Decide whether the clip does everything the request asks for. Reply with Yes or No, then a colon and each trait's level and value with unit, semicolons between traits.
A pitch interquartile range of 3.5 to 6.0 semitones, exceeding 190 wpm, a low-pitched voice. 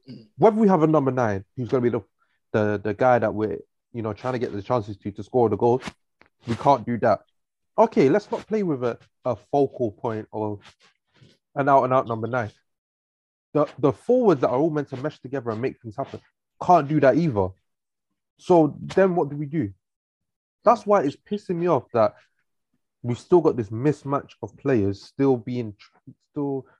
Yes: wide, 5.6 semitones; average, 200 wpm; low, 125 Hz